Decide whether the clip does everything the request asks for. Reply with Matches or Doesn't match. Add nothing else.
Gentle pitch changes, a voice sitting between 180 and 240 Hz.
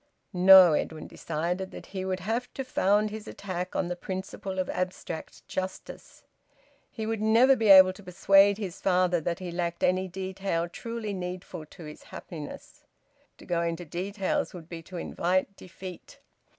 Matches